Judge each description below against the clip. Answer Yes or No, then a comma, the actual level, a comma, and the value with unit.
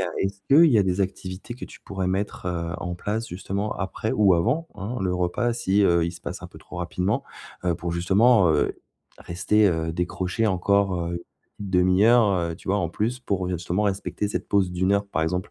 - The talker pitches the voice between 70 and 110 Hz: Yes, very low, 95 Hz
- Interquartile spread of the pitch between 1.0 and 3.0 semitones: Yes, average, 2.7 semitones